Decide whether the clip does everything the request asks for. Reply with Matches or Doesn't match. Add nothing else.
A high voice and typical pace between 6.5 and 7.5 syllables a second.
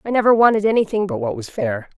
Matches